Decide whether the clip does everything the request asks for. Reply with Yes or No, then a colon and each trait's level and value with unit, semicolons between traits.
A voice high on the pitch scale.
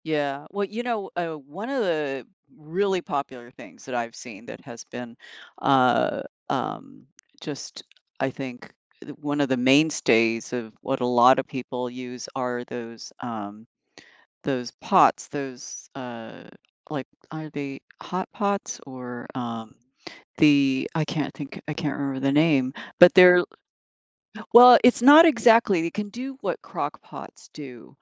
No: medium, 140 Hz